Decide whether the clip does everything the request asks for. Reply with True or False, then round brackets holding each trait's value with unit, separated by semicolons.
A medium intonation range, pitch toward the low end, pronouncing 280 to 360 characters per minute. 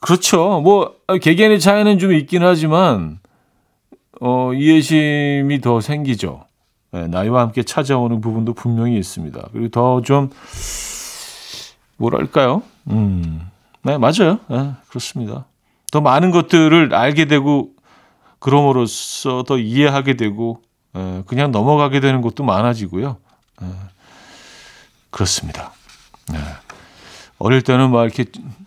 False (4.7 semitones; 130 Hz; 250 characters per minute)